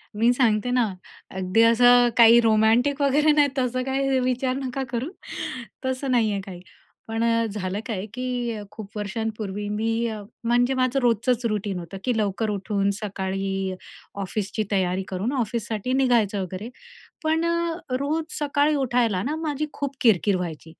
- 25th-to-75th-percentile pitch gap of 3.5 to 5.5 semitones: Yes, average, 4.1 semitones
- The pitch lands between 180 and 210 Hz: No, high, 230 Hz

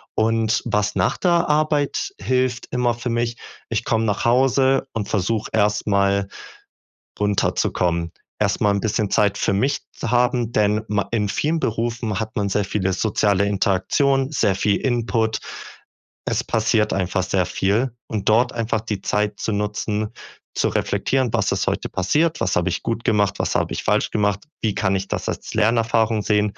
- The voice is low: Yes, low, 110 Hz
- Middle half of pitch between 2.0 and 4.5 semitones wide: Yes, average, 2.7 semitones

